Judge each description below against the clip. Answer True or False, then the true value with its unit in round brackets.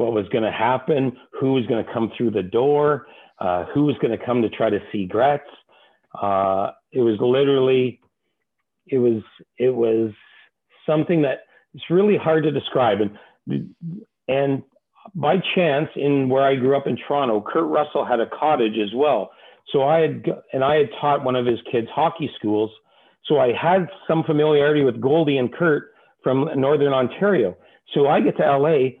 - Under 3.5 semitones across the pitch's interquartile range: False (4.1 semitones)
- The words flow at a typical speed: True (180 wpm)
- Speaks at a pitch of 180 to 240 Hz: False (135 Hz)